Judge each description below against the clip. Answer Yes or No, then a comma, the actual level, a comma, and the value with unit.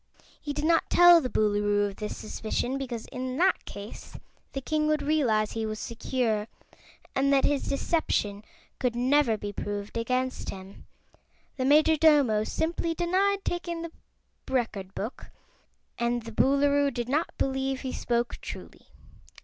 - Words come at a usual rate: Yes, average, 145 wpm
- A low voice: No, very high, 260 Hz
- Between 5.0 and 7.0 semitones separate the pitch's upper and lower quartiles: Yes, wide, 5.4 semitones